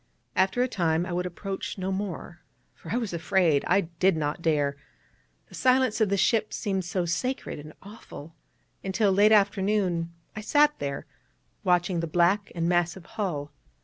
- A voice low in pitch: No, medium, 185 Hz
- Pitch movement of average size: Yes, average, 3.5 semitones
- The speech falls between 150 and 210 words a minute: Yes, average, 170 wpm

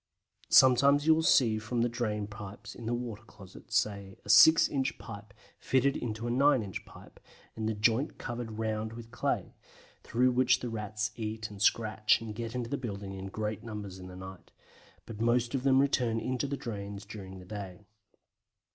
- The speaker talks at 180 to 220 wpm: Yes, average, 190 wpm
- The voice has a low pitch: Yes, low, 110 Hz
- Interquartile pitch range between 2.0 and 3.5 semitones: Yes, average, 2.8 semitones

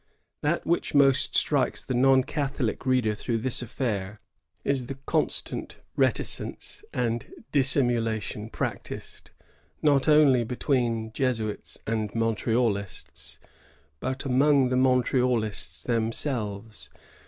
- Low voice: Yes, low, 125 Hz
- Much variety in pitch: No, average, 3.2 semitones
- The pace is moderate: No, slow, 100 wpm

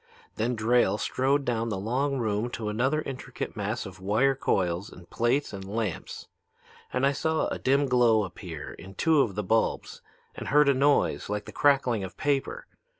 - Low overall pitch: Yes, low, 120 Hz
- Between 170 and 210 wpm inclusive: Yes, average, 180 wpm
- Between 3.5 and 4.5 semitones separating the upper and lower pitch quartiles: No, average, 5.0 semitones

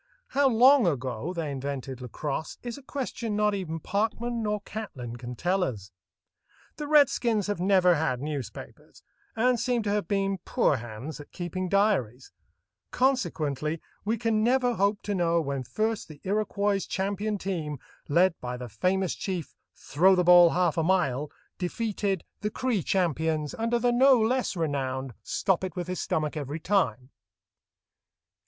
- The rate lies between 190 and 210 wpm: No, average, 155 wpm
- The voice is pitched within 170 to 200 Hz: Yes, medium, 185 Hz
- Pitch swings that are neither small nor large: No, wide, 6.3 semitones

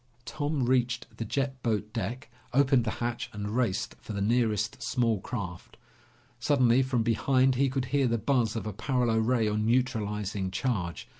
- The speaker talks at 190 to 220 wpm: No, average, 165 wpm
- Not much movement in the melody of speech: No, average, 3.2 semitones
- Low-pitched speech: Yes, low, 120 Hz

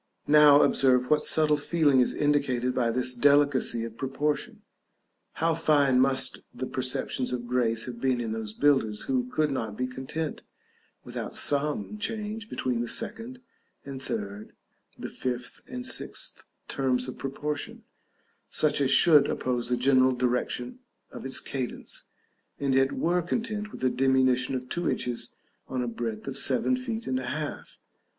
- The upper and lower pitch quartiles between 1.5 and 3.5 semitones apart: Yes, average, 3.2 semitones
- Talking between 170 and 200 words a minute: No, average, 155 wpm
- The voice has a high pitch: No, low, 130 Hz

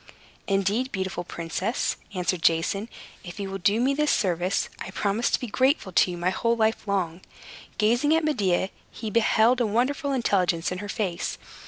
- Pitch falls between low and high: No, high, 200 Hz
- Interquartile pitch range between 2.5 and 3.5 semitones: No, average, 4.4 semitones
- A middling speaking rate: Yes, average, 175 wpm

